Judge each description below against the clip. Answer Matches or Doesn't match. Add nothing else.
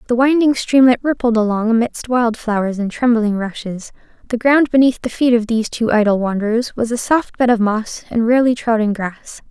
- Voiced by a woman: Matches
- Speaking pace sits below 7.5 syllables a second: Matches